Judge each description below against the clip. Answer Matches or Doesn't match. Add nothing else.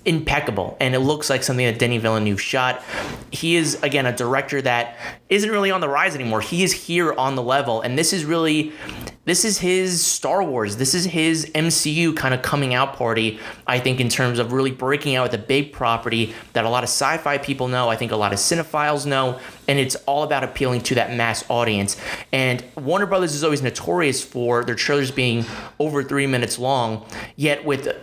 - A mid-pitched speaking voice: Doesn't match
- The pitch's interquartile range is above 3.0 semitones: Matches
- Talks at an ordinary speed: Doesn't match